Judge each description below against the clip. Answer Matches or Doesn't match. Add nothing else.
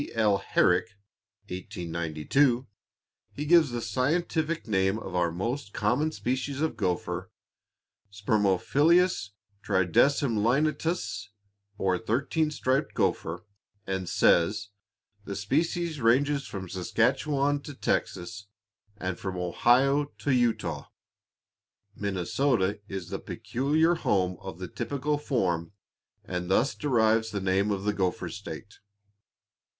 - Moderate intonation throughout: Doesn't match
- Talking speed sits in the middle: Doesn't match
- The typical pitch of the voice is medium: Doesn't match